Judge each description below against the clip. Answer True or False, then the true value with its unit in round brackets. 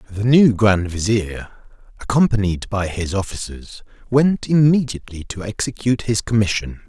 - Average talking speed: False (120 wpm)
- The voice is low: True (110 Hz)